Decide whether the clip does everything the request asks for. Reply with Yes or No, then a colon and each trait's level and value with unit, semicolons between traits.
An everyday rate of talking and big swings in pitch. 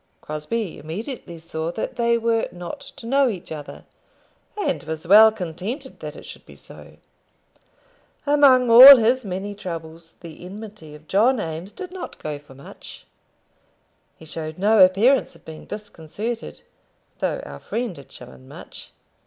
Yes: average, 150 wpm; wide, 6.5 semitones